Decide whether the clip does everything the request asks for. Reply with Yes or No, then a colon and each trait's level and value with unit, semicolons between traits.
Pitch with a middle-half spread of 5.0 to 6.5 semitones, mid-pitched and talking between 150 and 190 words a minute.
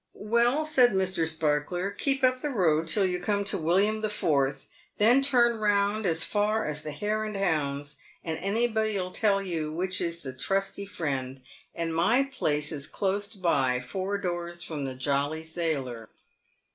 Yes: wide, 5.4 semitones; medium, 180 Hz; average, 170 wpm